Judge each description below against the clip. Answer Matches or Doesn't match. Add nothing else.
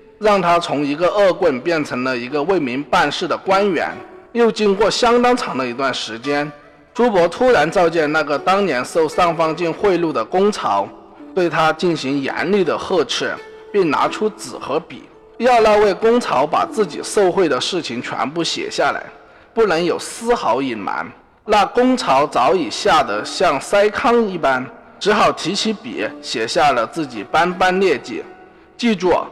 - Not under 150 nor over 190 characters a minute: Doesn't match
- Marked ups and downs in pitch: Matches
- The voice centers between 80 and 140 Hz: Doesn't match